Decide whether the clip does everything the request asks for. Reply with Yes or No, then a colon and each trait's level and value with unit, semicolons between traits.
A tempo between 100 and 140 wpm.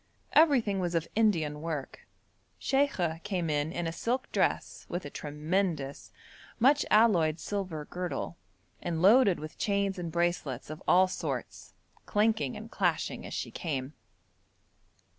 Yes: slow, 135 wpm